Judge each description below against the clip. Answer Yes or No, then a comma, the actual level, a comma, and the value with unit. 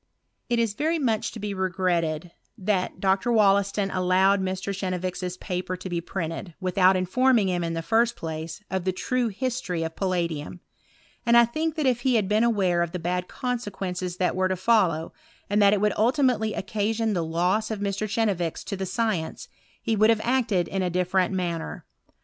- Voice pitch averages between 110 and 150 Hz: No, high, 190 Hz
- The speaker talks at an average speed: Yes, average, 185 wpm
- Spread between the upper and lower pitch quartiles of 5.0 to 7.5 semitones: No, average, 3.5 semitones